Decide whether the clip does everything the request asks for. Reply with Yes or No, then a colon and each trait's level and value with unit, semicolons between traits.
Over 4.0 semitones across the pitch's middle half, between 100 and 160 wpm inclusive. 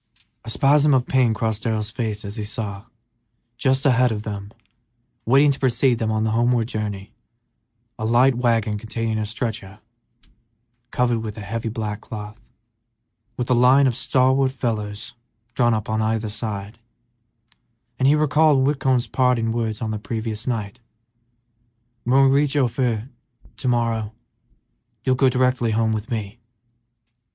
No: average, 2.8 semitones; average, 145 wpm